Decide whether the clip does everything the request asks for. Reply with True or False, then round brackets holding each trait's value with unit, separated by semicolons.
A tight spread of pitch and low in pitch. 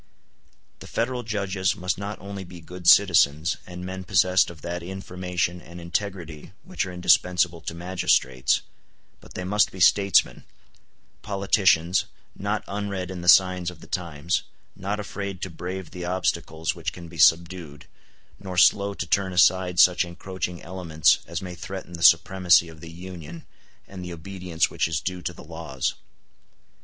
True (2.0 semitones; 90 Hz)